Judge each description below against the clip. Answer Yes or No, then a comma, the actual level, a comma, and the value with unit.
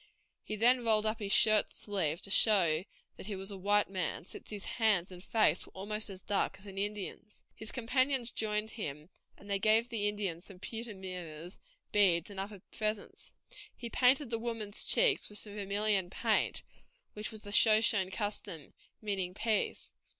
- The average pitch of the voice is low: No, high, 205 Hz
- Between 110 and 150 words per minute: No, average, 175 wpm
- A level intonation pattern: Yes, narrow, 2.3 semitones